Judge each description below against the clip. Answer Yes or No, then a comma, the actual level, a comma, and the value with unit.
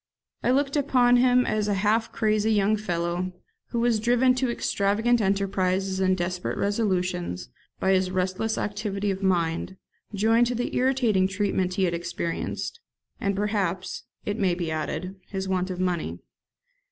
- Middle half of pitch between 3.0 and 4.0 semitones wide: Yes, average, 3.3 semitones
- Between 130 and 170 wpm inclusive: Yes, average, 155 wpm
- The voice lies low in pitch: No, high, 195 Hz